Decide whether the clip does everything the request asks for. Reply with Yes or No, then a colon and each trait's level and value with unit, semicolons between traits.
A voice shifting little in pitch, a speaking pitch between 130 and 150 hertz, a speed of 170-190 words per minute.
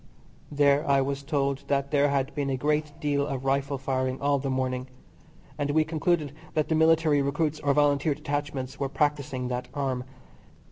Yes: narrow, 1.5 semitones; medium, 140 Hz; average, 175 wpm